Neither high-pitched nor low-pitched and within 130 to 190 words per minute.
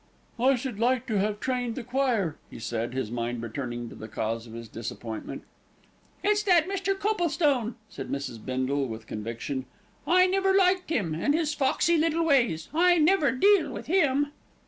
No: very high, 250 Hz; average, 175 wpm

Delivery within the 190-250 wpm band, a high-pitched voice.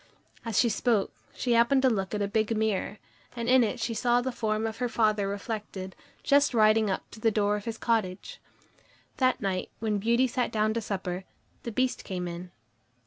Yes: average, 200 wpm; high, 220 Hz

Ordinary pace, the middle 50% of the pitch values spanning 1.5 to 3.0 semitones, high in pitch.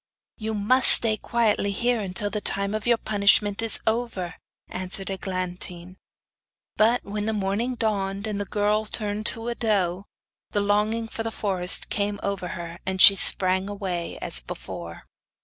Yes: average, 160 wpm; narrow, 2.6 semitones; high, 205 Hz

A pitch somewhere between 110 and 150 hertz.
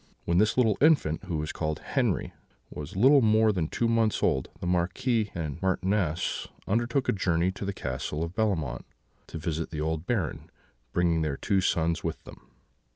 No: very low, 90 Hz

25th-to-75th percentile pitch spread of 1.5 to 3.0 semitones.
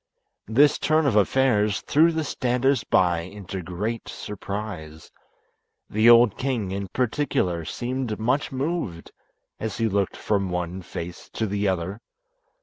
No: average, 5.2 semitones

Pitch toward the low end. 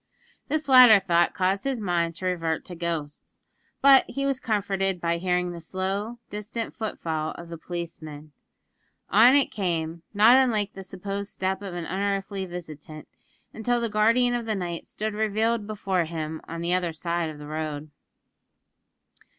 No: high, 190 Hz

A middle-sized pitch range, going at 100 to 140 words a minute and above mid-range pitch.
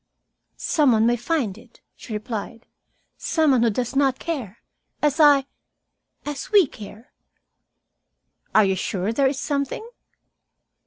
Yes: average, 4.6 semitones; slow, 135 wpm; very high, 250 Hz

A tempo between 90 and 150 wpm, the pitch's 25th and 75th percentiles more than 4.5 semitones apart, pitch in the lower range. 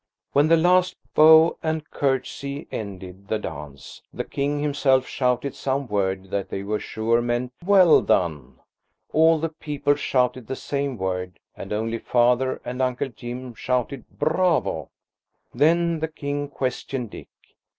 Yes: average, 140 wpm; average, 5.2 semitones; low, 130 Hz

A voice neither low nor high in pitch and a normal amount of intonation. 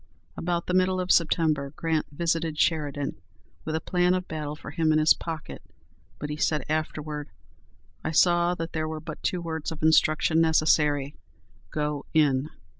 No: medium, 155 Hz; narrow, 1.7 semitones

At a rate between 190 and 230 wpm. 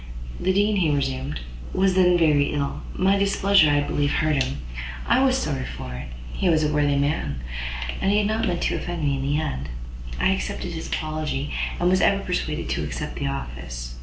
Yes: average, 195 wpm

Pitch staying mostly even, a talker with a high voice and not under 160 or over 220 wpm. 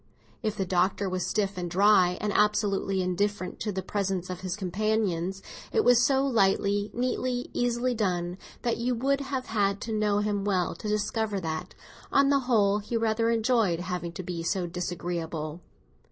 No: average, 3.8 semitones; high, 205 Hz; average, 170 wpm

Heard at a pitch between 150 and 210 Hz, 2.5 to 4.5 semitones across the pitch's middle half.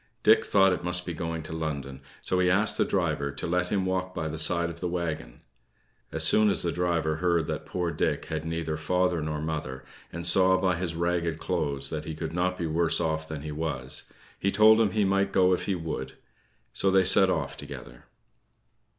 No: very low, 85 Hz; average, 2.8 semitones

